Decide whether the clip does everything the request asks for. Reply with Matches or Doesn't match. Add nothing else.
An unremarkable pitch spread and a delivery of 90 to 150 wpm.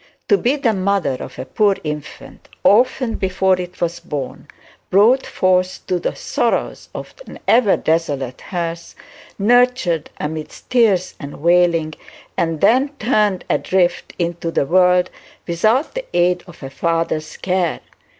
Matches